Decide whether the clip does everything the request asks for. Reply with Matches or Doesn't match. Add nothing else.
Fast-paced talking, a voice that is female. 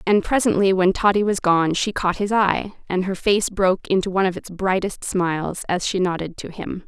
Matches